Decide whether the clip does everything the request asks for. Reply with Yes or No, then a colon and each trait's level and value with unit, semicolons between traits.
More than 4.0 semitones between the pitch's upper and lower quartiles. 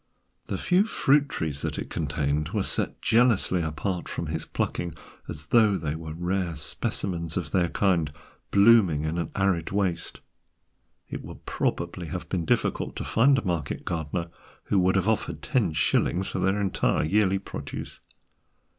No: average, 3.7 semitones